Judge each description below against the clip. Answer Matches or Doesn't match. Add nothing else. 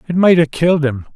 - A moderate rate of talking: Doesn't match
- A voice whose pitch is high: Doesn't match